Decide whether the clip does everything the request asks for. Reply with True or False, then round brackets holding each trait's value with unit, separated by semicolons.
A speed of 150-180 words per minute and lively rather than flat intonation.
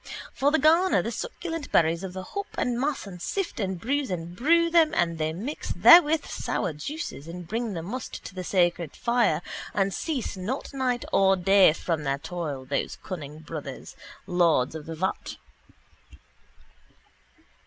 True (165 wpm; 8.6 semitones)